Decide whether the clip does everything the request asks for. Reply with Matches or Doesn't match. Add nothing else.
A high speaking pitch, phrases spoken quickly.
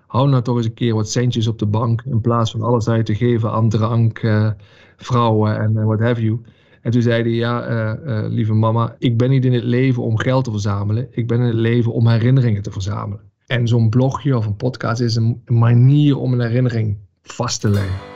Doesn't match